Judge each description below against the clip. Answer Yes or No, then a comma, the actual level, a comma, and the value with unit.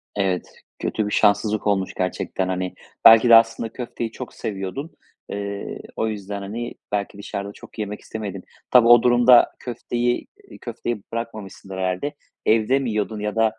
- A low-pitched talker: Yes, low, 110 Hz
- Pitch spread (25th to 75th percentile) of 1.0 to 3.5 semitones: Yes, average, 2.9 semitones